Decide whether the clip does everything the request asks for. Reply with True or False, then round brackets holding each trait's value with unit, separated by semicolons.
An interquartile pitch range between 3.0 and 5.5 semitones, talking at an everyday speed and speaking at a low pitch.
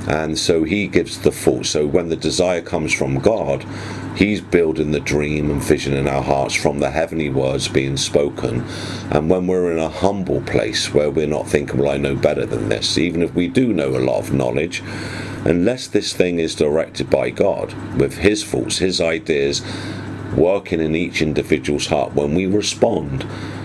True (4.6 semitones; 190 wpm; 85 Hz)